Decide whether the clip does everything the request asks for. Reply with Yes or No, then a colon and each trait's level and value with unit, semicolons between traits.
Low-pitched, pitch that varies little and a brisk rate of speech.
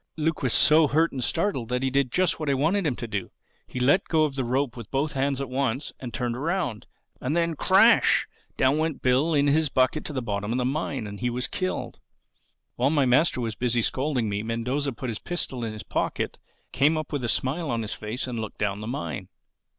No: low, 130 Hz; average, 4.3 semitones; fast, 225 wpm